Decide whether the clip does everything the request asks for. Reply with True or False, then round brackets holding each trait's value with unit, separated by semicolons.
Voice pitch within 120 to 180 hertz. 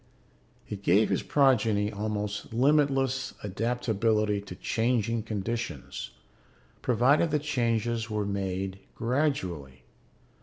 False (110 Hz)